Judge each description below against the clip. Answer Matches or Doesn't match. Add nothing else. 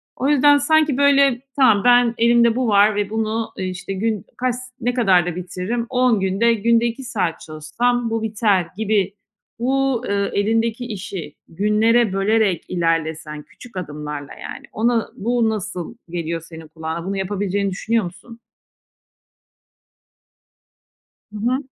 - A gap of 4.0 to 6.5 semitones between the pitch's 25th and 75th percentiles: Matches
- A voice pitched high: Matches